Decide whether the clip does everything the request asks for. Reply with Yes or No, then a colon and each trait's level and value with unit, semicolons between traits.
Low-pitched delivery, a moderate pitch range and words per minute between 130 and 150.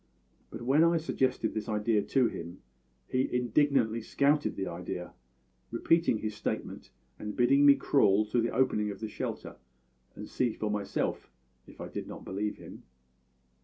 No: low, 115 Hz; average, 4.1 semitones; average, 160 wpm